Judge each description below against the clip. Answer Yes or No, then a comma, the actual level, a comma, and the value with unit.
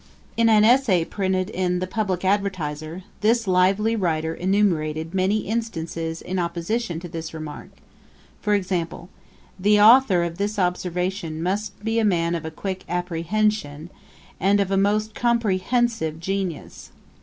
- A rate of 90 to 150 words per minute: Yes, average, 145 wpm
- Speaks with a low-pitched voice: No, medium, 185 Hz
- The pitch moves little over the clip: No, average, 3.8 semitones